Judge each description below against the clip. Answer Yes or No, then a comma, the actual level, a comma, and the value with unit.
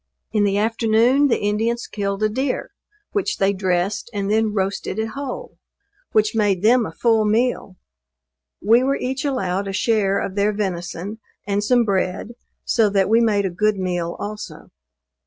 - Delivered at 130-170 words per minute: Yes, average, 165 wpm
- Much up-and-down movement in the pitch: No, narrow, 2.6 semitones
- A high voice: Yes, high, 210 Hz